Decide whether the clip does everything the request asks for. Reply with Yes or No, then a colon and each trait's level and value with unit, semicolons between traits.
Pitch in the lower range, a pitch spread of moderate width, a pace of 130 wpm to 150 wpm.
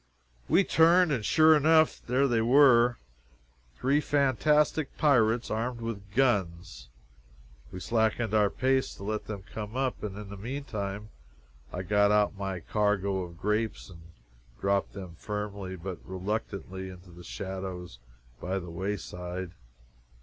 Yes: low, 105 Hz; average, 4.6 semitones; slow, 135 wpm